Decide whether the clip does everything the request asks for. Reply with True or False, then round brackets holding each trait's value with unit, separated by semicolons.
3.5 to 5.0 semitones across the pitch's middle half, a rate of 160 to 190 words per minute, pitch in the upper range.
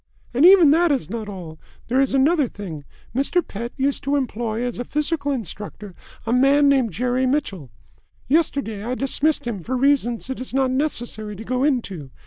True (4.1 semitones; 180 wpm; 255 Hz)